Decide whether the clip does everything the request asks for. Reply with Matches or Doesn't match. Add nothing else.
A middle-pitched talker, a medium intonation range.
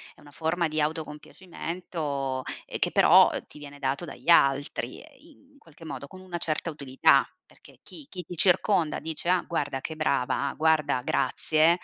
Matches